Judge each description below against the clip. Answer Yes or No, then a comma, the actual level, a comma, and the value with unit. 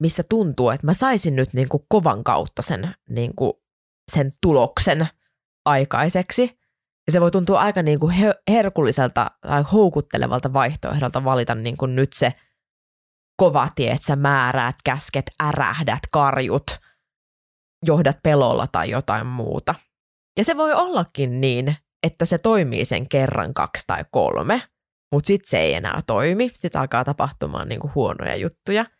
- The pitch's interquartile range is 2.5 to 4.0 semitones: No, wide, 5.6 semitones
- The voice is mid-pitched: Yes, medium, 145 Hz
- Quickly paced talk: No, average, 145 wpm